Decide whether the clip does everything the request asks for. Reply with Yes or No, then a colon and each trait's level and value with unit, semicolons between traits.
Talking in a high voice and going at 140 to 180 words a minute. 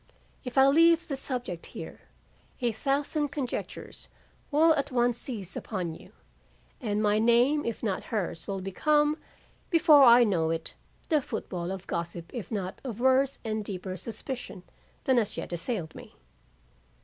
Yes: high, 235 Hz; average, 150 wpm